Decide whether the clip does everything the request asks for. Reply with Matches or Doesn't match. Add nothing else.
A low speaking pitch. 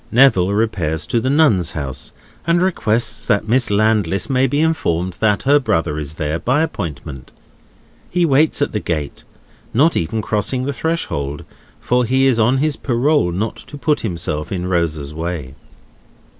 Matches